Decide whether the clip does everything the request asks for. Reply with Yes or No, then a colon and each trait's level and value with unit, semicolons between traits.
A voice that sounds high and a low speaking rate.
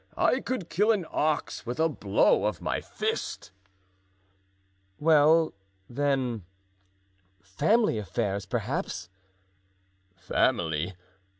No: low, 135 Hz; slow, 90 wpm